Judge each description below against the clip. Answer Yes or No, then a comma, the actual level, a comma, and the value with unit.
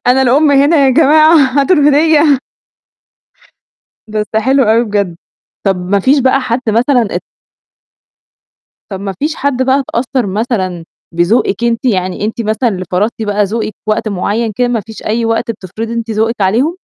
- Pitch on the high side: Yes, high, 230 Hz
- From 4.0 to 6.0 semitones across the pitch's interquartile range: Yes, average, 4.3 semitones